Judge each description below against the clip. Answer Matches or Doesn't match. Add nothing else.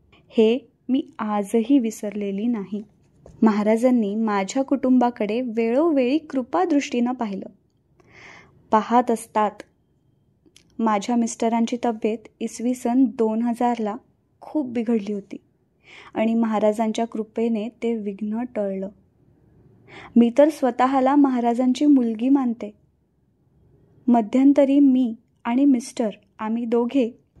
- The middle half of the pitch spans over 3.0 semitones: Doesn't match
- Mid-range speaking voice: Doesn't match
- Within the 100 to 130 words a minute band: Doesn't match